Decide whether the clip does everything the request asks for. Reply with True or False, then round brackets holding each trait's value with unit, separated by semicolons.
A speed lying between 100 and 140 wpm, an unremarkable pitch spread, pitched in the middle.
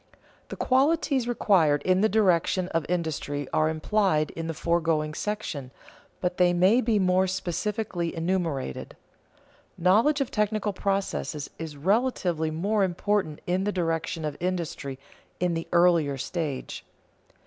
True (135 wpm; 4.3 semitones; 180 Hz)